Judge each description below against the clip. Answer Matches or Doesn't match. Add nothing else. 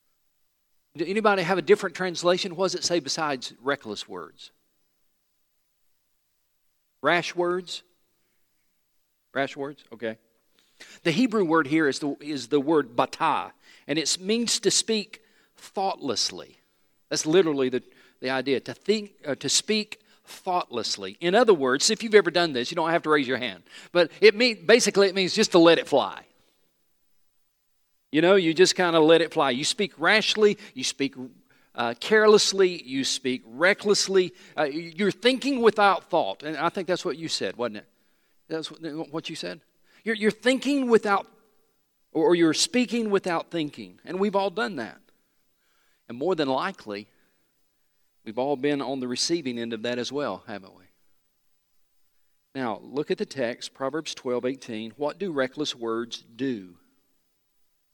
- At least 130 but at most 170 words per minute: Matches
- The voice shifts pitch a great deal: Matches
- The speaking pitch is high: Doesn't match